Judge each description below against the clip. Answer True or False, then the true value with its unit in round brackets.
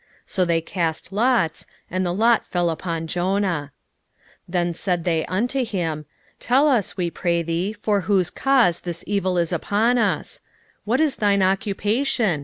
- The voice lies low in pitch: False (185 Hz)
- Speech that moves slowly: False (160 wpm)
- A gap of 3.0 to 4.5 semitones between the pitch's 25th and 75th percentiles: True (4.0 semitones)